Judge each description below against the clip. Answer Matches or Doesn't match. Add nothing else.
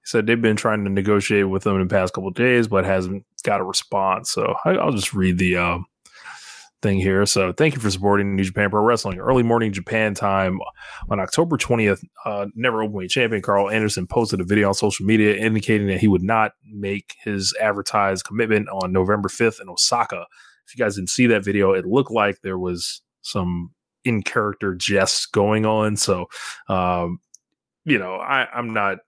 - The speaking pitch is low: Matches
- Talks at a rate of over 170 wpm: Matches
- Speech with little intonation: Matches